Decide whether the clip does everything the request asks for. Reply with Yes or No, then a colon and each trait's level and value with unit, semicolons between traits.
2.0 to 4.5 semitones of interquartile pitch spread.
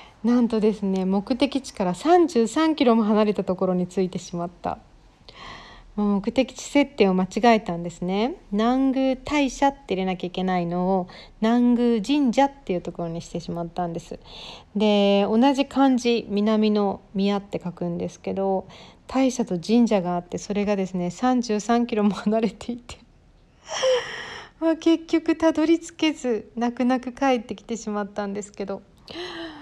No: wide, 5.5 semitones